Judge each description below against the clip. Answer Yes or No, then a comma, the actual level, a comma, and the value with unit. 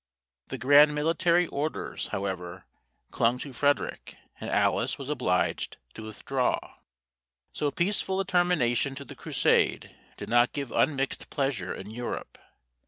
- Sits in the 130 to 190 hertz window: Yes, medium, 140 Hz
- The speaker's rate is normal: No, slow, 130 wpm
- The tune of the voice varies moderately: Yes, average, 4.2 semitones